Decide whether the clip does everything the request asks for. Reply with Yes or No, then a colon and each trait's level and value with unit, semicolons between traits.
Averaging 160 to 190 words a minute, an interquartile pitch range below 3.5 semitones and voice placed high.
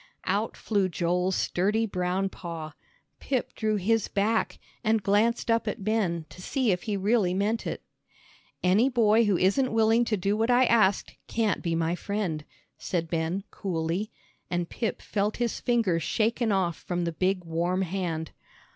No: average, 165 wpm; average, 4.0 semitones; high, 200 Hz